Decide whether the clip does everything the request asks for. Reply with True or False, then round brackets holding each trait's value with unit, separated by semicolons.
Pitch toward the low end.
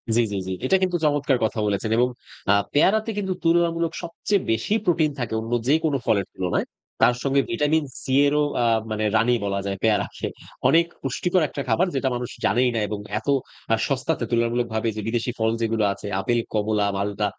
True (125 Hz)